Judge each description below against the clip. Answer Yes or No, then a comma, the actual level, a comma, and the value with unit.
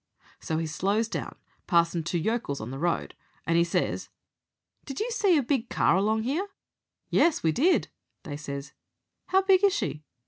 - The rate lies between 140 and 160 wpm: No, average, 175 wpm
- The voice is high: Yes, high, 200 Hz